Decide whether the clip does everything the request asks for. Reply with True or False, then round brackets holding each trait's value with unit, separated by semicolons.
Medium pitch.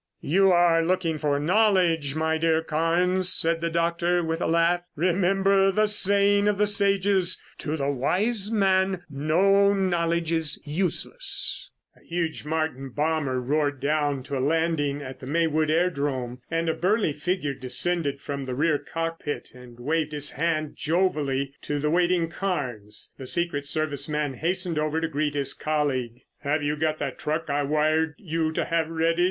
True (160 Hz)